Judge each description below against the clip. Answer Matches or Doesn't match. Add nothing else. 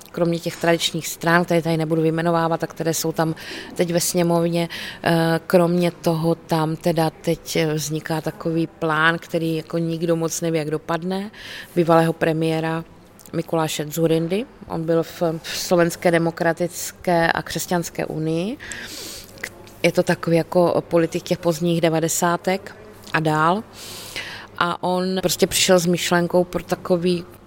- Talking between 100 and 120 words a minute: Doesn't match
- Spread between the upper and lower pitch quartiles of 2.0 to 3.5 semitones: Doesn't match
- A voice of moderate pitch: Matches